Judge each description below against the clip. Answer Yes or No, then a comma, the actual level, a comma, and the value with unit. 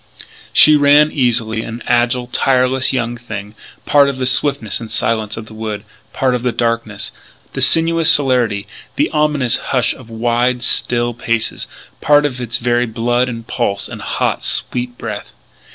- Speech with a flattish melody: Yes, narrow, 2.3 semitones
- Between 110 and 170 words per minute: Yes, average, 160 wpm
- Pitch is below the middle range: Yes, low, 120 Hz